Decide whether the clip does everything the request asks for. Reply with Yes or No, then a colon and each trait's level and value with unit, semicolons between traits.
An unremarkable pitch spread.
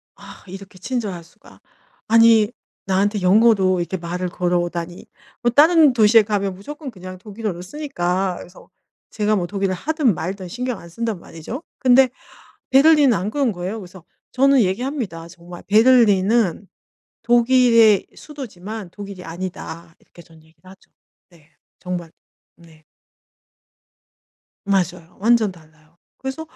Yes: average, 5.0 semitones